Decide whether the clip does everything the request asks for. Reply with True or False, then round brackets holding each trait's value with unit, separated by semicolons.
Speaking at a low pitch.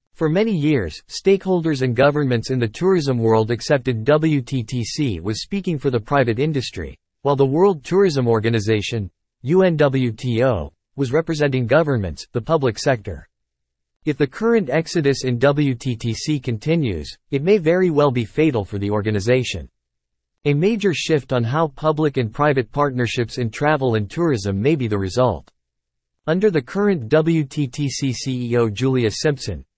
True (130 Hz)